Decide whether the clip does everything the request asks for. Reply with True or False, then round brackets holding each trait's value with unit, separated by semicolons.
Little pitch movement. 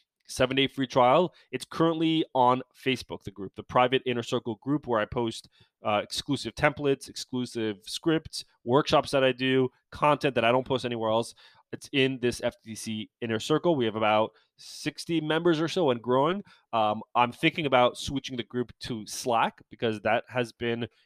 False (3.2 semitones)